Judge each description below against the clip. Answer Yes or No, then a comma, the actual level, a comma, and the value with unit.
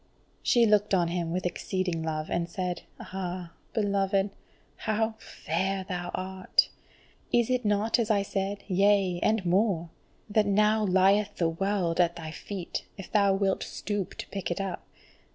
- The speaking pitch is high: Yes, high, 195 Hz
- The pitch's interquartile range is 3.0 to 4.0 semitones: No, narrow, 2.6 semitones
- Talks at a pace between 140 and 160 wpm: Yes, average, 155 wpm